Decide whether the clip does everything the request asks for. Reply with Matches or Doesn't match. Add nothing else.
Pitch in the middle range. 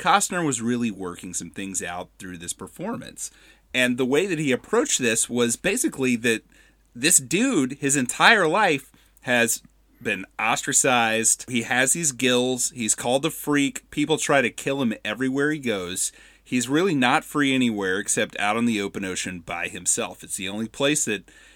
Doesn't match